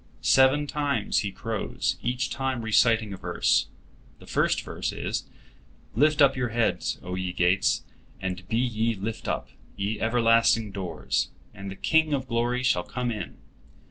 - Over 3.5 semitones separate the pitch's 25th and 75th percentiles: Yes, average, 4.2 semitones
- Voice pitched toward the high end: No, low, 115 Hz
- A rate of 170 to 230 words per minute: No, average, 155 wpm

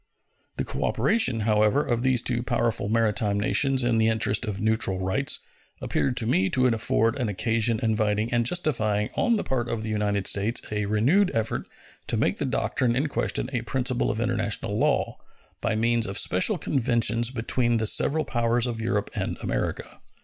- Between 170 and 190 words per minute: Yes, average, 175 wpm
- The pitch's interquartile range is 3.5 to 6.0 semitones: No, narrow, 2.5 semitones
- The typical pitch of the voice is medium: No, low, 115 Hz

